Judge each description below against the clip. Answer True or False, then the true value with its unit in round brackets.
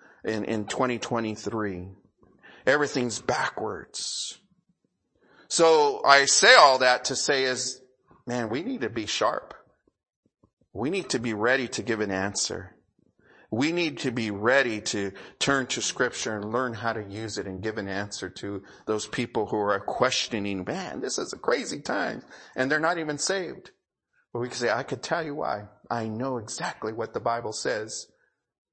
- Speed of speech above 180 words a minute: False (165 wpm)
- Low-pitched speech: True (120 Hz)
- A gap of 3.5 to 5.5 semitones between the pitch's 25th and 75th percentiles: True (3.8 semitones)